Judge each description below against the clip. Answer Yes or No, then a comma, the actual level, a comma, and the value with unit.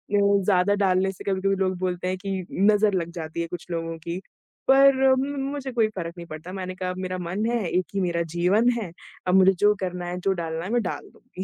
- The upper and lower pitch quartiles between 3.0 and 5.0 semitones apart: No, narrow, 2.4 semitones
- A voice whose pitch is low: No, medium, 185 Hz